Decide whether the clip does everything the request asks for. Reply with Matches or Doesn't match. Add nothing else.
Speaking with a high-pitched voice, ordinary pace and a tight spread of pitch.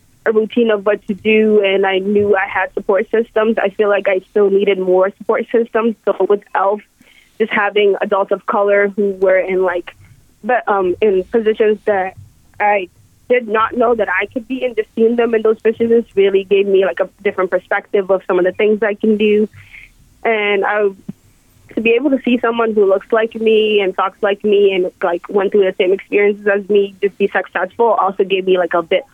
Doesn't match